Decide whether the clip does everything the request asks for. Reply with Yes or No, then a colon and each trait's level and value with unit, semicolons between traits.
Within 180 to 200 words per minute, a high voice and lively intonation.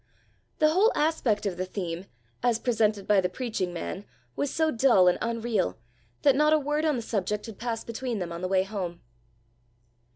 Yes: average, 190 wpm; high, 220 Hz; wide, 5.7 semitones